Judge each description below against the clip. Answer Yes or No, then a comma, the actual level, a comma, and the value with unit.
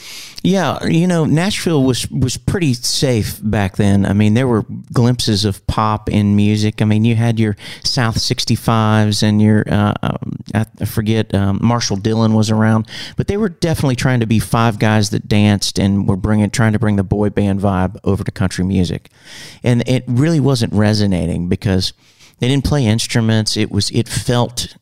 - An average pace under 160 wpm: No, average, 175 wpm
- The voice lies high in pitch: No, low, 110 Hz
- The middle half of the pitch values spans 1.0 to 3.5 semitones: Yes, average, 2.9 semitones